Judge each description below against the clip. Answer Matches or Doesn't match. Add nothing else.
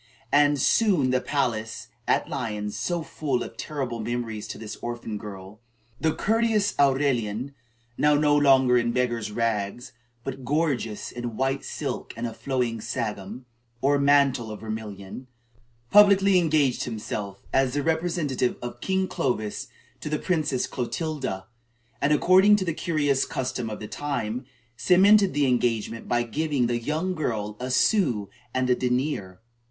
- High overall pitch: Doesn't match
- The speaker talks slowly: Doesn't match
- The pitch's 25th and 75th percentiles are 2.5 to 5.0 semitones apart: Matches